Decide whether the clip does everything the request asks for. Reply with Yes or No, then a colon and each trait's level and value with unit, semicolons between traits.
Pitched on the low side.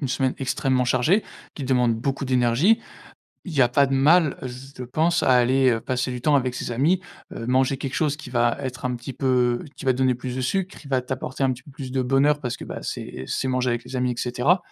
Yes: low, 130 Hz